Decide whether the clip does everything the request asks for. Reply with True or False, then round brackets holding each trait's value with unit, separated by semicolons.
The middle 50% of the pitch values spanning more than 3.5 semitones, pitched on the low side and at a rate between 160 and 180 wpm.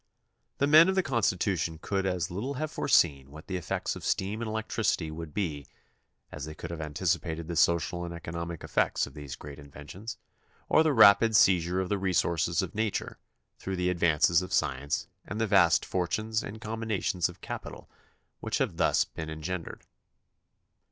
True (4.7 semitones; 90 Hz; 170 wpm)